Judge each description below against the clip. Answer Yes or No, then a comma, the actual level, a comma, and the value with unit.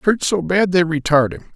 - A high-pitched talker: No, medium, 165 Hz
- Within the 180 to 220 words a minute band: No, fast, 230 wpm